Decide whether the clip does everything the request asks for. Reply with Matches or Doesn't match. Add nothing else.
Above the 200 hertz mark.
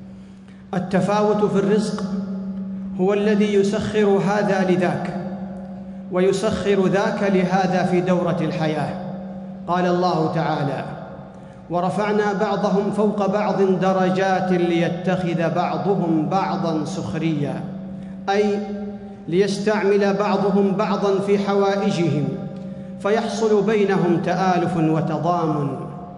Doesn't match